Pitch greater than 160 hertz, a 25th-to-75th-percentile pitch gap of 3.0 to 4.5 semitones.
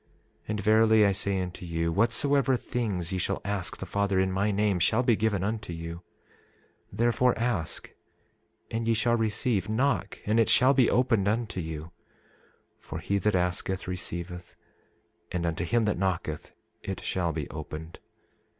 No: low, 100 Hz; average, 4.1 semitones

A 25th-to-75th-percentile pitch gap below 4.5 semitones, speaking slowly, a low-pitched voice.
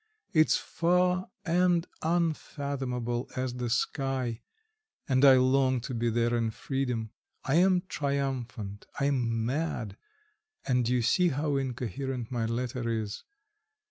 Yes: average, 3.3 semitones; slow, 125 wpm; low, 130 Hz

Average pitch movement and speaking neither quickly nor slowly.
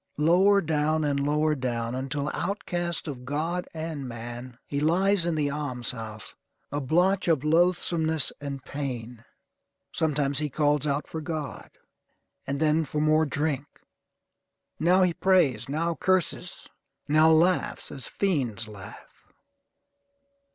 No: average, 3.3 semitones; slow, 130 wpm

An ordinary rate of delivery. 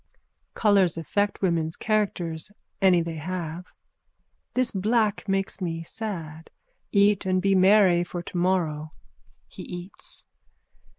No: slow, 110 wpm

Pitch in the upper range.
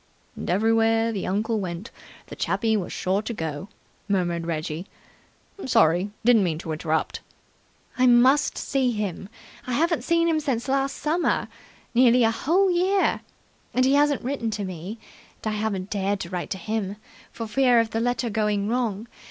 Yes: high, 225 Hz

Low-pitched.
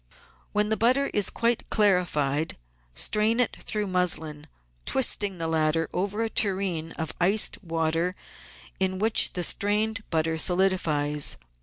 No: medium, 185 Hz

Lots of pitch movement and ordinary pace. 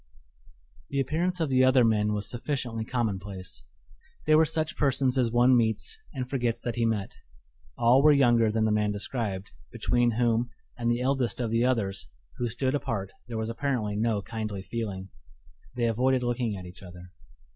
No: average, 3.4 semitones; average, 175 wpm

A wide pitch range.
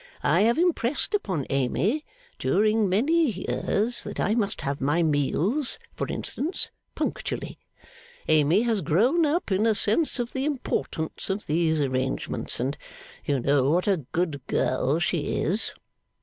Yes: wide, 8.1 semitones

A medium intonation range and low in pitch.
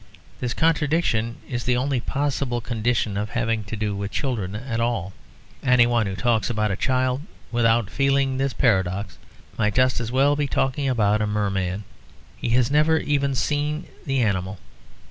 Yes: average, 4.3 semitones; low, 120 Hz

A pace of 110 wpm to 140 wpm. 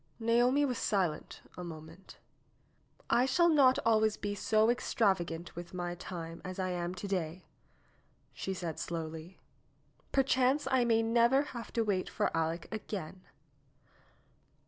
Yes: slow, 135 wpm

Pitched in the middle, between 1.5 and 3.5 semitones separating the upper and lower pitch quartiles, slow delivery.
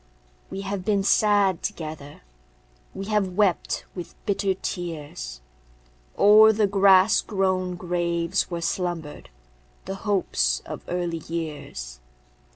Yes: medium, 180 Hz; average, 3.1 semitones; slow, 110 wpm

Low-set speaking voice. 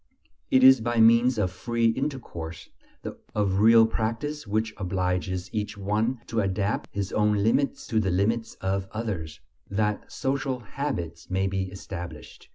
Yes: low, 105 Hz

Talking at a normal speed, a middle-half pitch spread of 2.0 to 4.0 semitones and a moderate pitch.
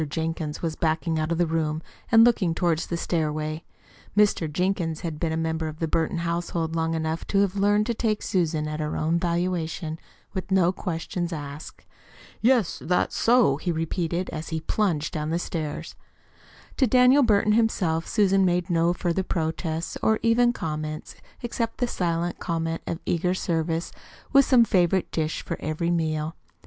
Yes: average, 170 wpm; average, 3.0 semitones; medium, 170 Hz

